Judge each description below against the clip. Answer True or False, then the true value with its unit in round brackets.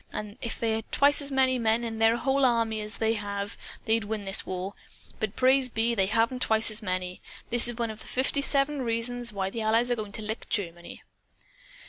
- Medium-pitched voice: False (225 Hz)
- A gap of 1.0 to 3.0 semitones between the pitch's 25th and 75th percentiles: True (2.5 semitones)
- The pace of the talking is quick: True (215 wpm)